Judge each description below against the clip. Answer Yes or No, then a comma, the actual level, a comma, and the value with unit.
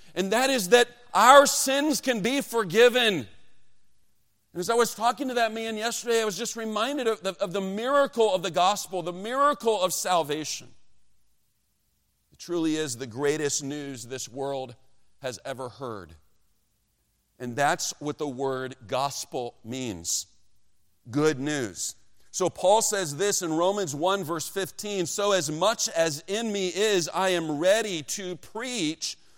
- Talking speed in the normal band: Yes, average, 155 wpm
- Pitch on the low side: No, medium, 175 Hz